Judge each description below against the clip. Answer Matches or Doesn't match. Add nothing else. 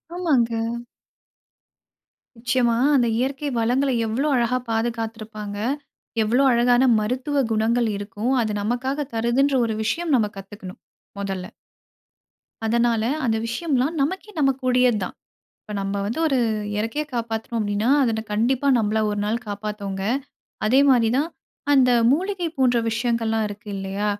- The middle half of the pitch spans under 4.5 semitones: Matches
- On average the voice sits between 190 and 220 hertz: Doesn't match